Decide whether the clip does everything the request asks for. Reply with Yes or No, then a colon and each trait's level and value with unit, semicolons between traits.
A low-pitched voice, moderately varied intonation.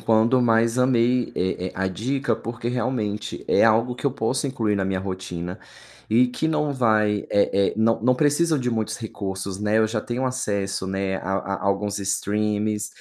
Yes: low, 110 Hz; average, 3.8 semitones